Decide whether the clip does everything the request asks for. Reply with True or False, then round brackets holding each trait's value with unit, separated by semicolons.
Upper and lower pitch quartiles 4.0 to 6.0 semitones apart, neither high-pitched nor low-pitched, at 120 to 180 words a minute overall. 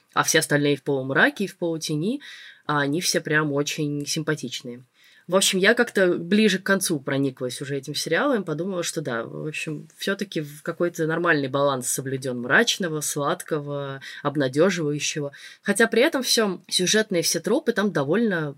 True (4.7 semitones; 160 Hz; 155 wpm)